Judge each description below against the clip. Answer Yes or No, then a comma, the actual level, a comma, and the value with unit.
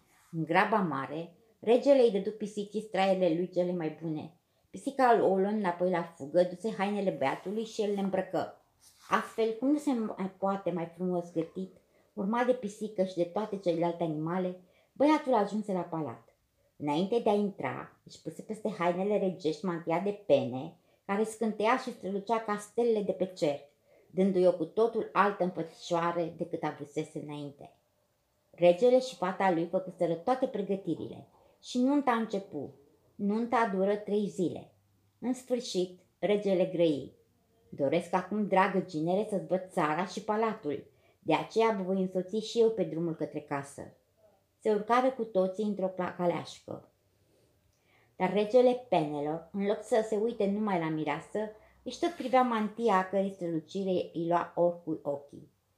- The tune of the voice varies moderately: Yes, average, 4.3 semitones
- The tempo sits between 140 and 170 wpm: Yes, average, 155 wpm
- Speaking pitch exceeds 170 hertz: Yes, medium, 185 Hz